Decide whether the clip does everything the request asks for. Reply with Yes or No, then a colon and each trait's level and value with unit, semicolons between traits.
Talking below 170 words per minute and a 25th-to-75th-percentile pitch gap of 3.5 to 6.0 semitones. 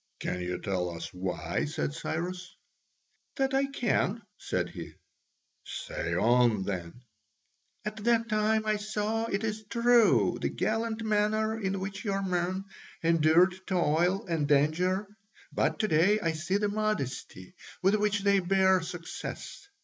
Yes: average, 140 wpm; wide, 5.4 semitones